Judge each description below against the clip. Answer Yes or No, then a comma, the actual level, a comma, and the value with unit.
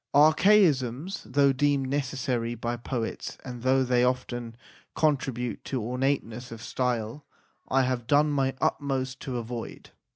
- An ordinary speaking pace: No, slow, 130 wpm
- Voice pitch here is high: No, low, 130 Hz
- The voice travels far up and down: No, narrow, 2.6 semitones